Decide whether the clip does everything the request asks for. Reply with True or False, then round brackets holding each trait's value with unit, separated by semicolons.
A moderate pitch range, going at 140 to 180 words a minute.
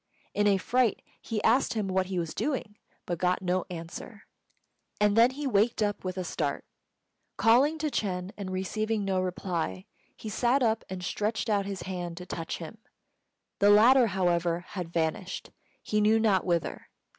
True (3.6 semitones; 170 wpm)